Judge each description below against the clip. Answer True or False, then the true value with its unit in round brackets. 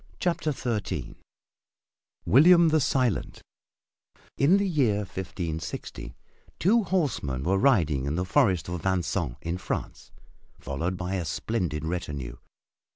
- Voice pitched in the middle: False (95 Hz)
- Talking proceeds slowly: True (115 wpm)